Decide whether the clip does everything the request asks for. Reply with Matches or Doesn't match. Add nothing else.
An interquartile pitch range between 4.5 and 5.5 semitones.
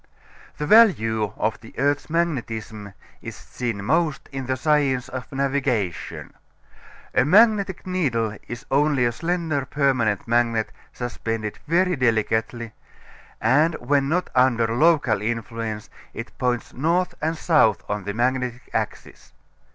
Matches